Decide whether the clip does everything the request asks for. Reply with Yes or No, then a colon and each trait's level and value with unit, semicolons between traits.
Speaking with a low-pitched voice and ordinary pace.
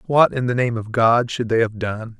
No: low, 120 Hz; fast, 275 wpm